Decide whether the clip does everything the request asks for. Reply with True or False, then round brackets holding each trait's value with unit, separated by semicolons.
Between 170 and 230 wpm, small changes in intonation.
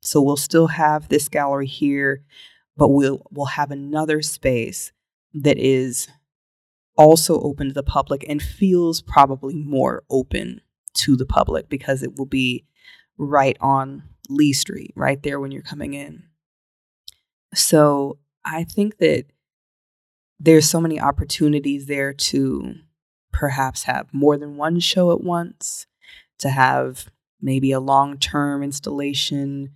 False (135 wpm; 2.0 semitones)